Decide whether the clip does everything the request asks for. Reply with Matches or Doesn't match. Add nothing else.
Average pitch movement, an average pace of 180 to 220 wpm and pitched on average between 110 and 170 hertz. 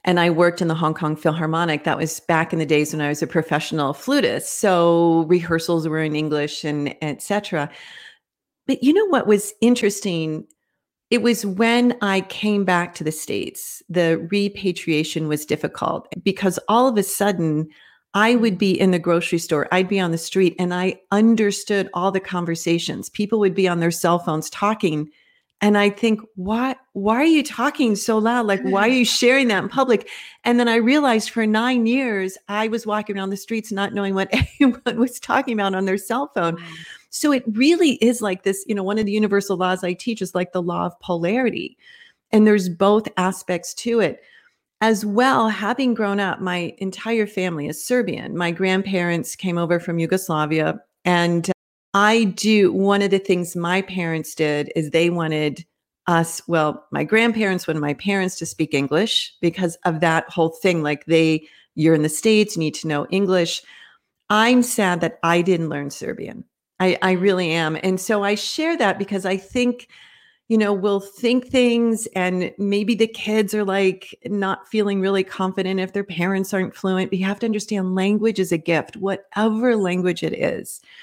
Doesn't match